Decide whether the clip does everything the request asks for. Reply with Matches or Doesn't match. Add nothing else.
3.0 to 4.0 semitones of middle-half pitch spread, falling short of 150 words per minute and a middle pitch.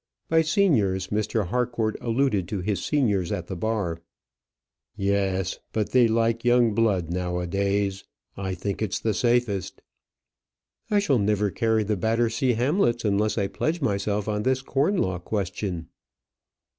Doesn't match